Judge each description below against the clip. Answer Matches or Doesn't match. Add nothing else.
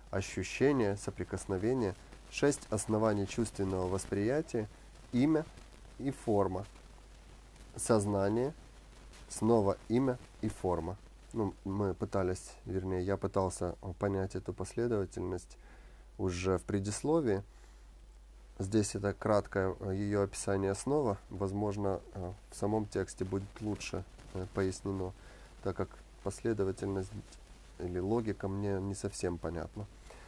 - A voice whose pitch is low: Matches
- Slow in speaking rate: Matches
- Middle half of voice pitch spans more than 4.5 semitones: Doesn't match